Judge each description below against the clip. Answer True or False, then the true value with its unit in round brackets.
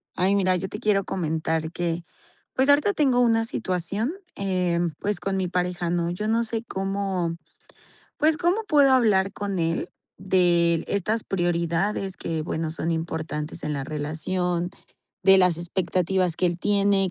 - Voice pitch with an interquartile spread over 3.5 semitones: False (3.1 semitones)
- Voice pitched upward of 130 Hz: True (185 Hz)